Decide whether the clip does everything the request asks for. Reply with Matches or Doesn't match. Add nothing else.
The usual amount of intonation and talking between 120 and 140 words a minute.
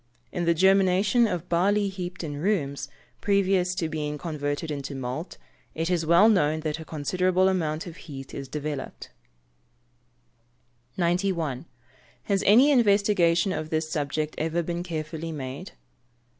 Matches